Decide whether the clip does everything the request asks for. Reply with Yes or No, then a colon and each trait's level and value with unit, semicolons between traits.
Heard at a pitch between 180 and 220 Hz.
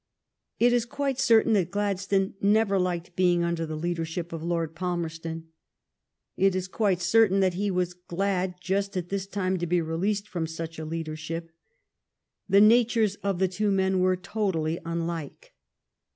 Yes: medium, 185 Hz